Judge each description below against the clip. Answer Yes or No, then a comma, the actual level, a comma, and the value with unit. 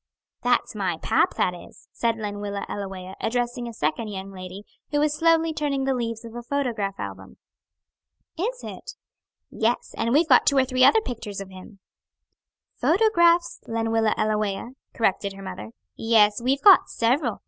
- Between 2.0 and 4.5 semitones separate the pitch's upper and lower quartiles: No, wide, 5.4 semitones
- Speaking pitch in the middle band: No, high, 230 Hz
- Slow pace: No, average, 160 wpm